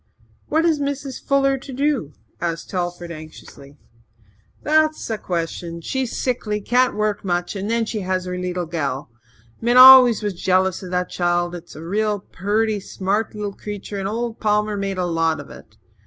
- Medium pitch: No, high, 200 Hz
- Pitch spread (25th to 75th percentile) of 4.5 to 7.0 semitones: Yes, average, 5.0 semitones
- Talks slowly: No, average, 170 wpm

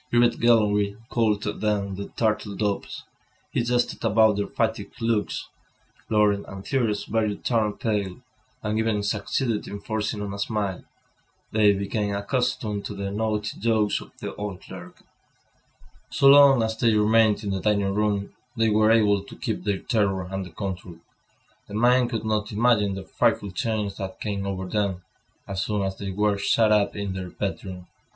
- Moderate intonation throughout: No, narrow, 1.8 semitones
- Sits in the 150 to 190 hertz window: No, low, 105 Hz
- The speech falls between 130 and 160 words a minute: No, average, 170 wpm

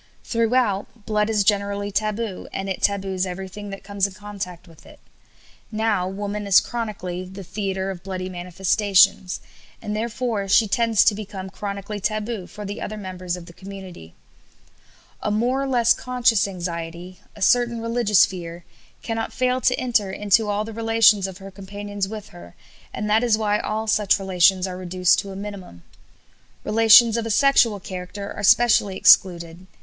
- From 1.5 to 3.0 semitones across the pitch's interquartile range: Yes, average, 2.7 semitones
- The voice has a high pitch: Yes, high, 200 Hz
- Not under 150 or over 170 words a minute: Yes, average, 165 wpm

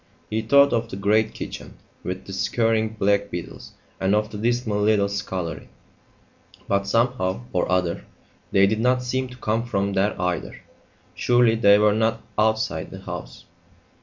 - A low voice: Yes, low, 105 Hz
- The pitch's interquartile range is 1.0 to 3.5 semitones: Yes, narrow, 2.5 semitones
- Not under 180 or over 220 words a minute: No, average, 160 wpm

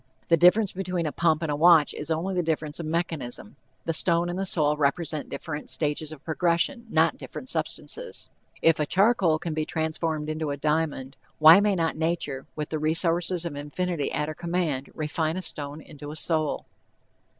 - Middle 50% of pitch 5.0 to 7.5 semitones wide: No, narrow, 2.4 semitones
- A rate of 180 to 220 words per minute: Yes, average, 185 wpm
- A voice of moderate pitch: Yes, medium, 160 Hz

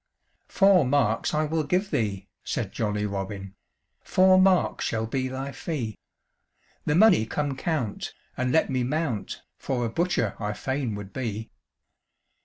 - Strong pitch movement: Yes, wide, 6.4 semitones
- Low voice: Yes, low, 130 Hz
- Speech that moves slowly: No, average, 145 wpm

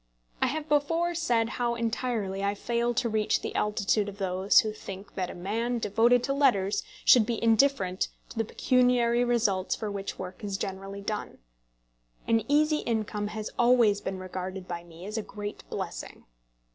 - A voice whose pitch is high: Yes, high, 215 Hz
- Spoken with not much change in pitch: No, average, 3.6 semitones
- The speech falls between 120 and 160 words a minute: No, average, 170 wpm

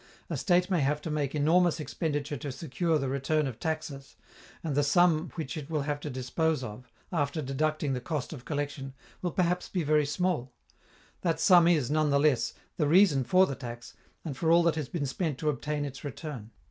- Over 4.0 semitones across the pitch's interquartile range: No, average, 3.1 semitones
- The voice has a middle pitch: Yes, medium, 150 Hz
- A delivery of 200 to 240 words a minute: Yes, fast, 205 wpm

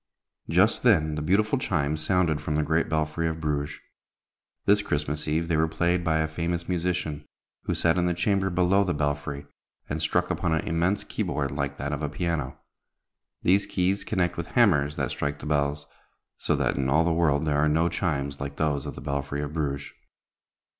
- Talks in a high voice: No, very low, 80 Hz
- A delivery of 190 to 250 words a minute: Yes, average, 195 wpm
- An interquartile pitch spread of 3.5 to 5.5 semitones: No, average, 3.1 semitones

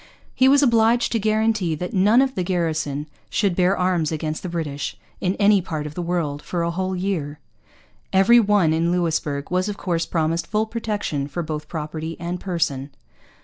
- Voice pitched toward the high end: No, medium, 175 Hz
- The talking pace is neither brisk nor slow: Yes, average, 185 wpm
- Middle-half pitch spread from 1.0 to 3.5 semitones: No, average, 4.3 semitones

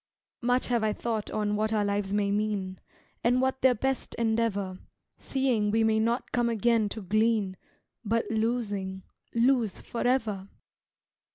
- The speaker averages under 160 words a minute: Yes, average, 145 wpm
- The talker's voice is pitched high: Yes, high, 220 Hz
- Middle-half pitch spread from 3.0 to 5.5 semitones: No, narrow, 2.5 semitones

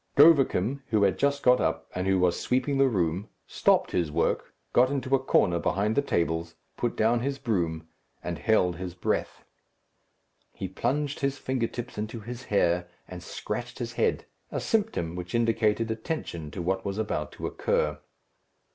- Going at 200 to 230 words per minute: No, average, 165 wpm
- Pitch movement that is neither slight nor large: No, wide, 6.5 semitones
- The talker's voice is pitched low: Yes, low, 110 Hz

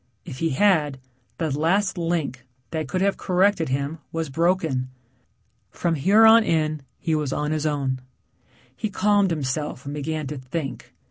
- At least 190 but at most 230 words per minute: No, average, 155 wpm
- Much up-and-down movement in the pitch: No, average, 4.3 semitones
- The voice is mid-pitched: Yes, medium, 155 Hz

